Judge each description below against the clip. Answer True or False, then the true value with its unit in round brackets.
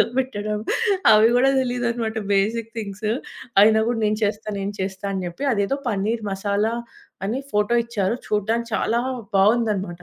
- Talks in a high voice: True (215 Hz)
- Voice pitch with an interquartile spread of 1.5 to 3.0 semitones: True (2.6 semitones)